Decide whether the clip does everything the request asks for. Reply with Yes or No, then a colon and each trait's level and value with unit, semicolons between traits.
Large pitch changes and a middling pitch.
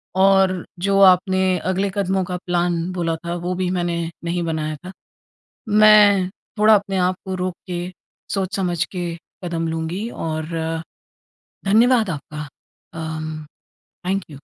No: narrow, 2.4 semitones; medium, 180 Hz